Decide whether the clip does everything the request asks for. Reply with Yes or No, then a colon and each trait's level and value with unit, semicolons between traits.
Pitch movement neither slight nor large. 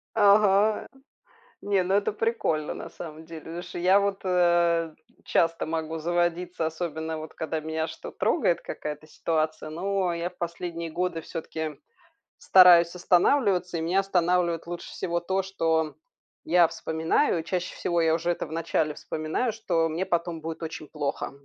No: narrow, 2.2 semitones